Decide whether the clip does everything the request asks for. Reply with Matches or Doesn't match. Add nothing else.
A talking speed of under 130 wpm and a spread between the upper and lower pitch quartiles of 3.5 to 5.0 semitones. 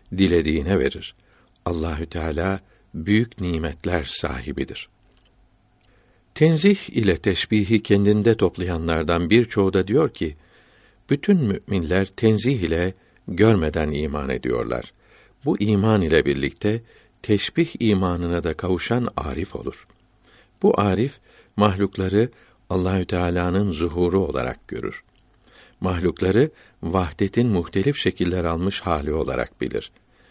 Matches